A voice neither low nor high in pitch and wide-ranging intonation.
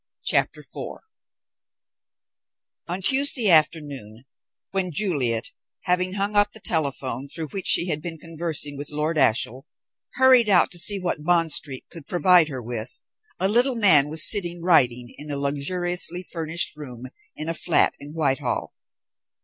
No: medium, 160 Hz; average, 4.4 semitones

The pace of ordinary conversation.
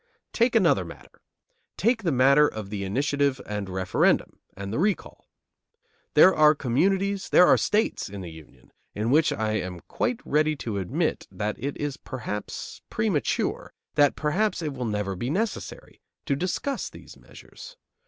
Yes: average, 155 wpm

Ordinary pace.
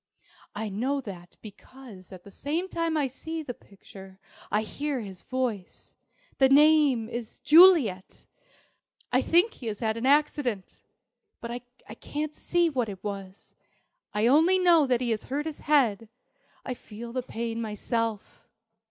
Yes: average, 150 wpm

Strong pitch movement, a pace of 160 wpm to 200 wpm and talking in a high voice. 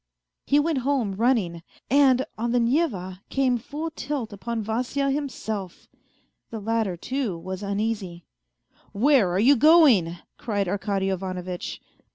No: wide, 5.9 semitones; average, 145 wpm; high, 225 Hz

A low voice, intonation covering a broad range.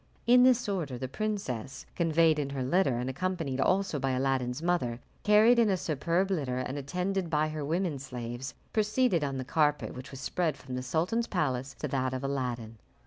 No: medium, 145 Hz; wide, 5.9 semitones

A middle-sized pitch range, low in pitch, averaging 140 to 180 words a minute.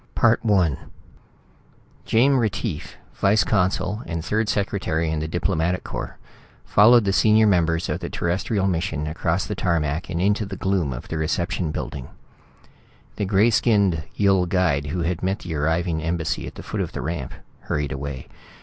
Yes: average, 3.8 semitones; very low, 90 Hz; average, 160 wpm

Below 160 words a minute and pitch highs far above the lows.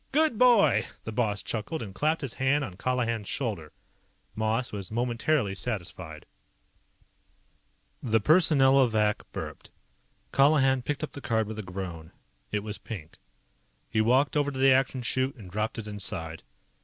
No: average, 145 wpm; average, 4.7 semitones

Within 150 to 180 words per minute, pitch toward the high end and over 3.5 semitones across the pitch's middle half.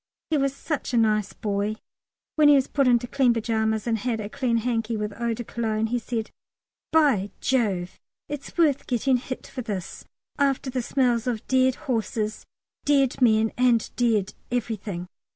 No: average, 170 wpm; high, 235 Hz; average, 3.1 semitones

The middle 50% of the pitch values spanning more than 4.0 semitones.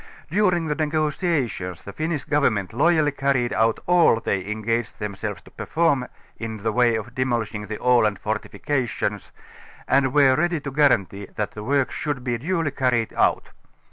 Yes: average, 5.3 semitones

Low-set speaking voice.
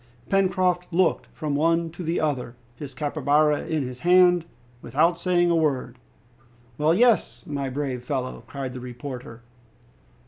No: medium, 150 Hz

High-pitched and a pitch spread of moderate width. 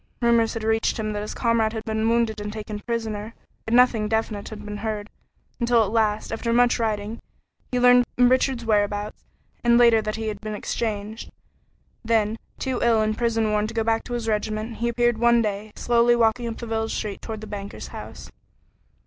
No: high, 225 Hz; narrow, 1.7 semitones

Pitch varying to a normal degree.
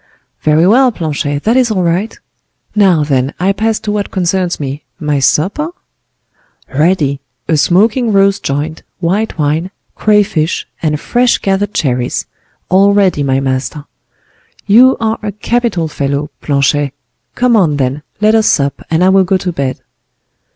No: wide, 6.1 semitones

